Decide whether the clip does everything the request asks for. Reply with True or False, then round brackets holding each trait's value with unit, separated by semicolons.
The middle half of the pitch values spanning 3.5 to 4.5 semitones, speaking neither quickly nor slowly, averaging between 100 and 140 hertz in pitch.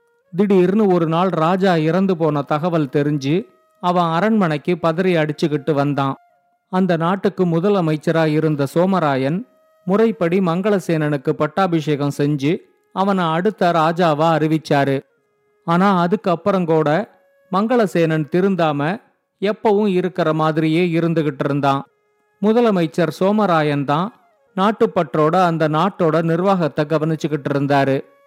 False (4.0 semitones; 95 wpm; 170 Hz)